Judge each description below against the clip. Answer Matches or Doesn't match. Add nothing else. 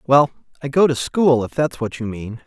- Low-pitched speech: Matches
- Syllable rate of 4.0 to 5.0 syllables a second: Matches